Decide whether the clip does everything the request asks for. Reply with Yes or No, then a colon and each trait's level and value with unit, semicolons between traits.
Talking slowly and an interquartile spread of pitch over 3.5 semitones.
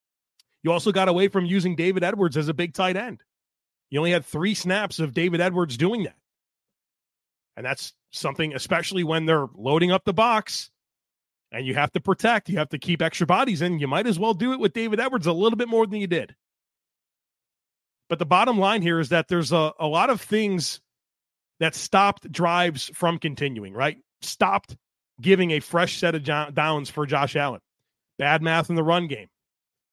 No: average, 190 wpm; average, 3.9 semitones